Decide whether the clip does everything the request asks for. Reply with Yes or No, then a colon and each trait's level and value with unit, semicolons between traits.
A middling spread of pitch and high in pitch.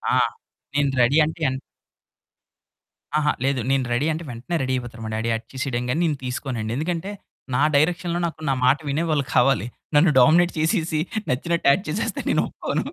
No: average, 4.5 semitones; medium, 140 Hz